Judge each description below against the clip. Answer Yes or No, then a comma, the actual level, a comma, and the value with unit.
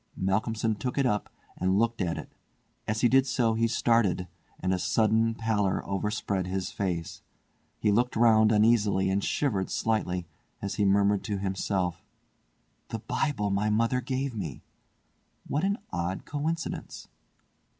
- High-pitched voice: No, low, 105 Hz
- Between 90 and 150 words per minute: Yes, average, 145 wpm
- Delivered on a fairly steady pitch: No, average, 3.3 semitones